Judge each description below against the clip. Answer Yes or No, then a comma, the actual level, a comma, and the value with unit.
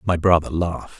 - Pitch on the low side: Yes, very low, 85 Hz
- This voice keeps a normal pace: Yes, average, 180 wpm